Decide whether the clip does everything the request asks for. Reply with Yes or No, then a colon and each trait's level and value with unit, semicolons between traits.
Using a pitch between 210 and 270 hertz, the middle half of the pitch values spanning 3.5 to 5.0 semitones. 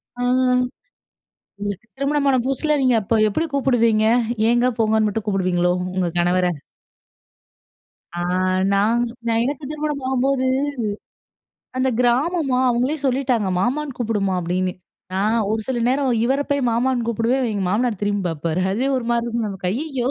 Yes: high, 235 Hz; average, 4.5 semitones